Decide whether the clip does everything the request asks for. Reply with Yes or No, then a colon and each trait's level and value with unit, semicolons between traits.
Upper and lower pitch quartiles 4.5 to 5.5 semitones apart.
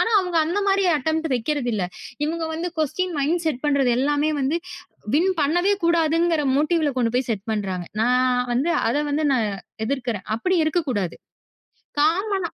Yes: average, 5.0 semitones